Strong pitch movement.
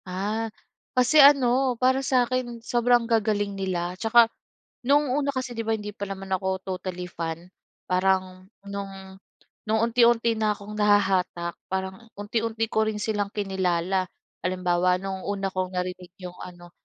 No: average, 3.6 semitones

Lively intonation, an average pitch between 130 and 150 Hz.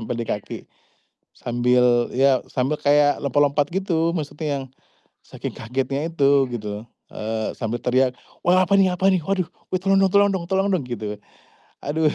Yes: wide, 6.3 semitones; medium, 140 Hz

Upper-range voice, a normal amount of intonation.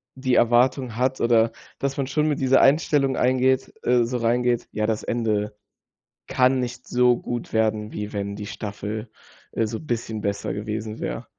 No: low, 120 Hz; average, 3.1 semitones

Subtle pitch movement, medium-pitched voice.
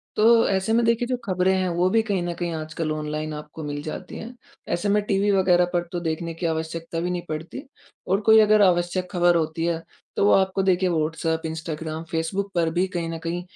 No: average, 3.0 semitones; medium, 175 Hz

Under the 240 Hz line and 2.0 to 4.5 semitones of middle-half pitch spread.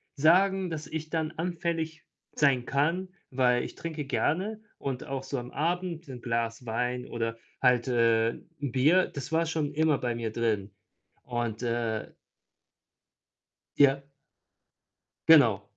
No: medium, 140 Hz; average, 5.2 semitones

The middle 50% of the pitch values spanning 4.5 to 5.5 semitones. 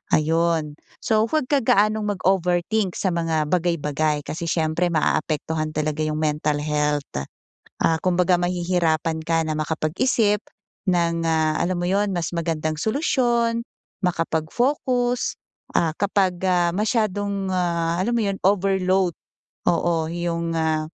No: average, 3.8 semitones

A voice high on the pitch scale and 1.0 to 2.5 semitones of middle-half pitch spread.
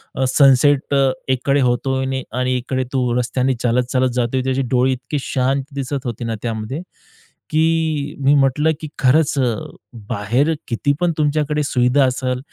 No: low, 130 Hz; narrow, 1.9 semitones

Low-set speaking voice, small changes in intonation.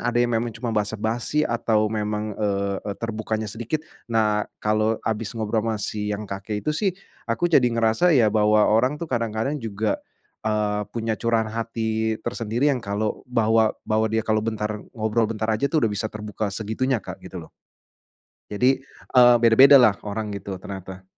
Yes: low, 110 Hz; narrow, 1.6 semitones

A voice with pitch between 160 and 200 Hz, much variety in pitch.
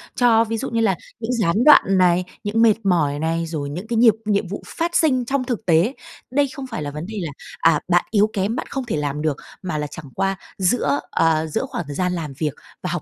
Yes: high, 190 Hz; wide, 6.1 semitones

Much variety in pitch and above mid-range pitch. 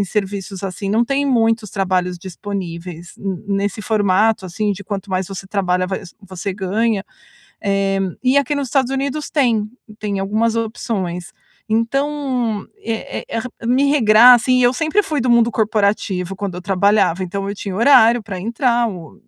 No: average, 3.7 semitones; high, 210 Hz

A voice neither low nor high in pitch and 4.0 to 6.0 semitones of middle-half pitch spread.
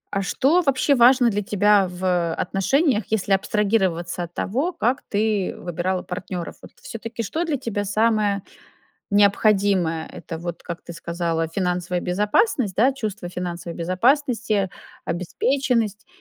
No: high, 200 Hz; average, 4.5 semitones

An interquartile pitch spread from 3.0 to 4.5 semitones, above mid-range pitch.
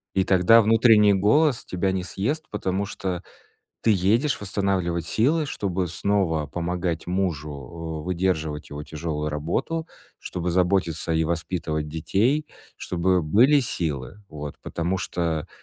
No: average, 4.0 semitones; very low, 90 Hz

